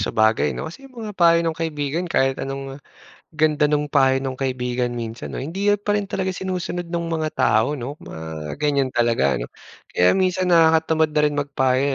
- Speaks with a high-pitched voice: No, medium, 145 Hz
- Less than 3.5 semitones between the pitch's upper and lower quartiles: No, average, 4.7 semitones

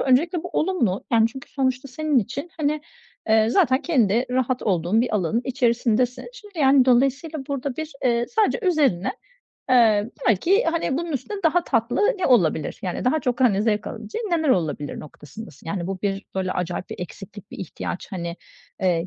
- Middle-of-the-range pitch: No, very high, 250 Hz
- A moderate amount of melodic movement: No, wide, 6.8 semitones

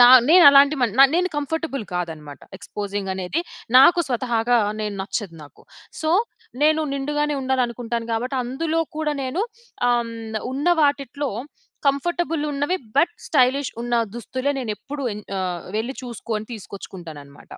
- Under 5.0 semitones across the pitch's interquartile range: No, wide, 5.4 semitones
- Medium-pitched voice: No, very high, 255 Hz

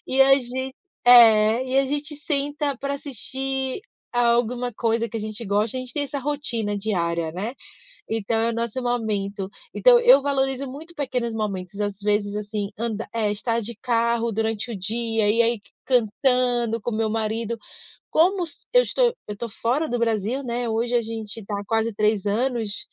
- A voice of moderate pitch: No, high, 230 Hz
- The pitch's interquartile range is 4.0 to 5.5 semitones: No, average, 3.4 semitones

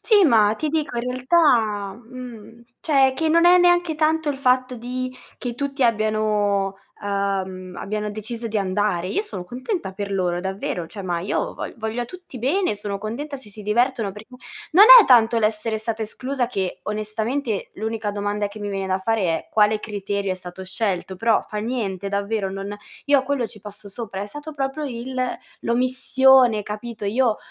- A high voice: Yes, high, 220 Hz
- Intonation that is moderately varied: Yes, average, 4.1 semitones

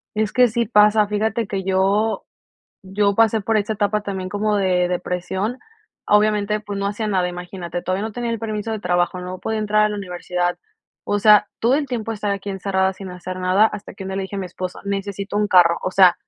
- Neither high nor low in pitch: No, high, 200 Hz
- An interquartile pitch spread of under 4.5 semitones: Yes, narrow, 2.4 semitones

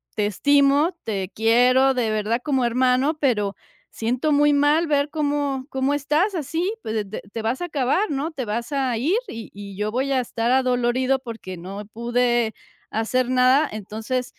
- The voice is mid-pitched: No, very high, 255 Hz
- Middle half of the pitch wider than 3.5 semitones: Yes, average, 4.2 semitones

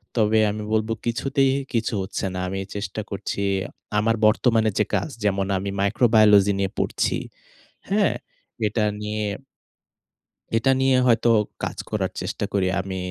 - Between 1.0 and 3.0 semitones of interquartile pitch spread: Yes, narrow, 2.4 semitones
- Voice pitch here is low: Yes, low, 110 Hz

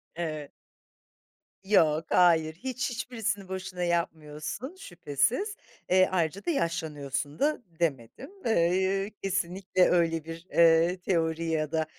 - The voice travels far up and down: No, average, 3.3 semitones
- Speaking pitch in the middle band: Yes, medium, 170 Hz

